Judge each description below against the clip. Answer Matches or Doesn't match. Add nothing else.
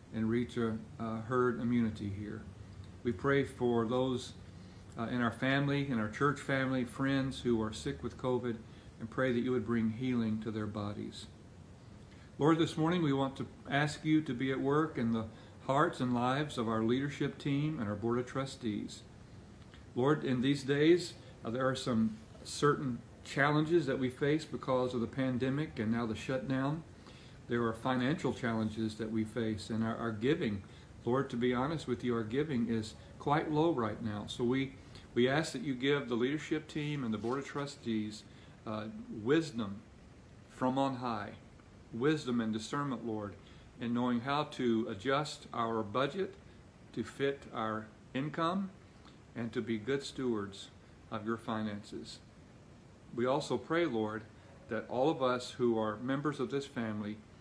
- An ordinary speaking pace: Matches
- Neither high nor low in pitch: Doesn't match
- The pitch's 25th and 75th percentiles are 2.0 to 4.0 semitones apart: Matches